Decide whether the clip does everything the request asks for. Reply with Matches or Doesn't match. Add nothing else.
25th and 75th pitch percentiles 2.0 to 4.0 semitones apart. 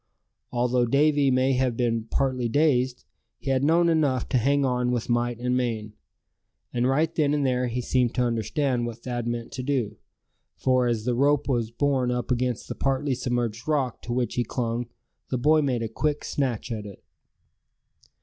Matches